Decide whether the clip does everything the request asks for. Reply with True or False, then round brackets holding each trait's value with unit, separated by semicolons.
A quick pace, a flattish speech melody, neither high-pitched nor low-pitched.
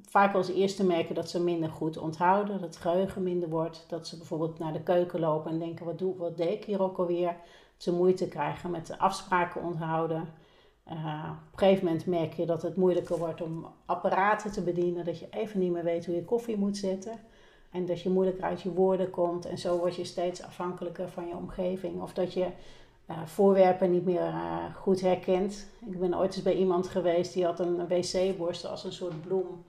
True (220 wpm; 1.7 semitones; 180 Hz)